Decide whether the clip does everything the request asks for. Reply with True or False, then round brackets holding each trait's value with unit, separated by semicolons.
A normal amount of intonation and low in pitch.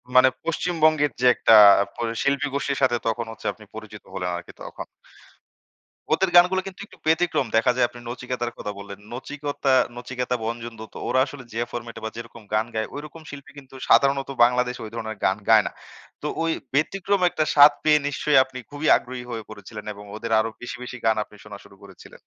True (4.2 semitones; 125 Hz)